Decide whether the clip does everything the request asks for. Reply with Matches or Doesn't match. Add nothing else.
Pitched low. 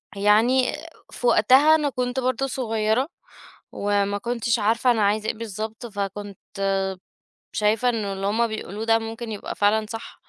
Doesn't match